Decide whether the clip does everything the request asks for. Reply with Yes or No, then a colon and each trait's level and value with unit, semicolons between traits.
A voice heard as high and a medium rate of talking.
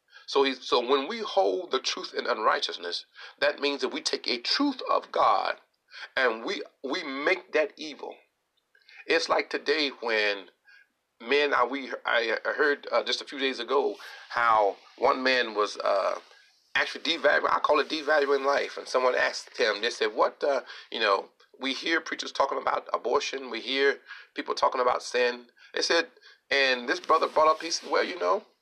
Yes: very high, 280 Hz; average, 180 wpm